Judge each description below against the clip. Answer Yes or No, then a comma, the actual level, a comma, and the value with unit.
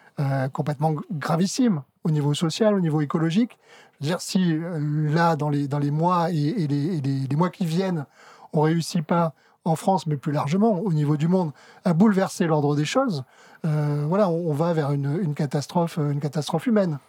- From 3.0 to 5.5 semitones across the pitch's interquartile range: Yes, average, 3.3 semitones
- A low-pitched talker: No, medium, 160 Hz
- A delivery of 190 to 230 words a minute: Yes, average, 205 wpm